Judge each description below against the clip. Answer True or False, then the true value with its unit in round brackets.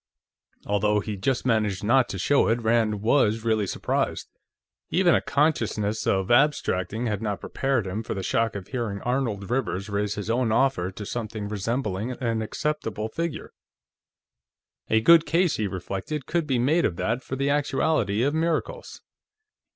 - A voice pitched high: False (115 Hz)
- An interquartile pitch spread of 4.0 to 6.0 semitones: True (4.7 semitones)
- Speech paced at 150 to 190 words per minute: True (160 wpm)